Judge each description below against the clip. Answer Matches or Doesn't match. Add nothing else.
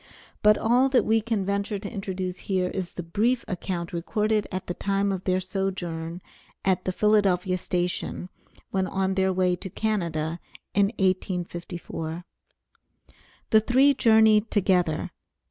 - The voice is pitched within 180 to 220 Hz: Matches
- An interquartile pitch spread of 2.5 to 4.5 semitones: Matches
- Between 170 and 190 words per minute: Doesn't match